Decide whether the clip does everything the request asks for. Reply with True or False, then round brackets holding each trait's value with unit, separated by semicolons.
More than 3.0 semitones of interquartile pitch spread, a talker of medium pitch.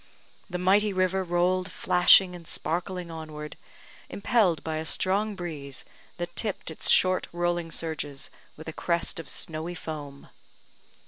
False (2.6 semitones; 175 Hz)